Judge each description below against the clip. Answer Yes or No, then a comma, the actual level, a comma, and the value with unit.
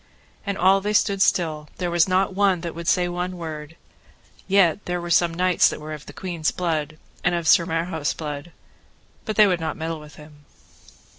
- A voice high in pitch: No, medium, 170 Hz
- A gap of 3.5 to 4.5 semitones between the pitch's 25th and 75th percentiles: No, narrow, 2.6 semitones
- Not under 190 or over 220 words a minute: Yes, average, 200 wpm